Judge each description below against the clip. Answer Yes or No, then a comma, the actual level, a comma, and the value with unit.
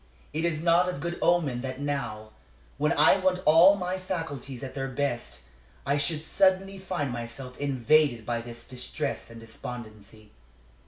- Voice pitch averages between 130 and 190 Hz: Yes, medium, 140 Hz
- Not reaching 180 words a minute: Yes, average, 155 wpm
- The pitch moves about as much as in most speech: No, wide, 6.1 semitones